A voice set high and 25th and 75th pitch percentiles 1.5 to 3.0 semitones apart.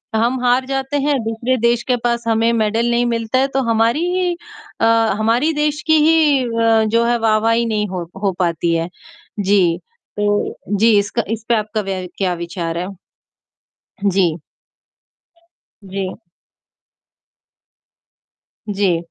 No: high, 225 Hz; average, 3.4 semitones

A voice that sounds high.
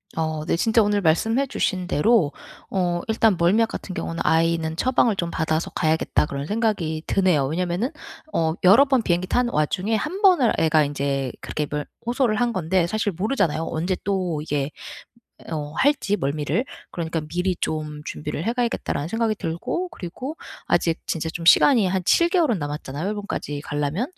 No: medium, 180 Hz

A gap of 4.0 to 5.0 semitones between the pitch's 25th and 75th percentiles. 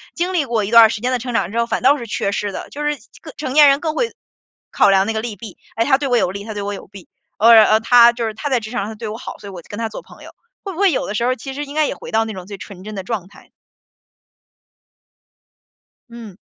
Yes: average, 4.4 semitones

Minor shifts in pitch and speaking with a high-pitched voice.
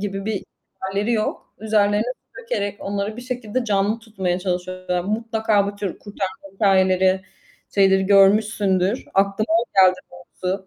Yes: narrow, 2.2 semitones; high, 200 Hz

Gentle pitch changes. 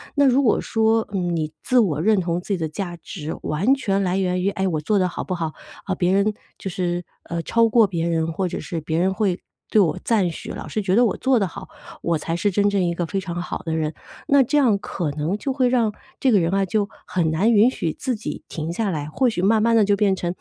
No: average, 4.1 semitones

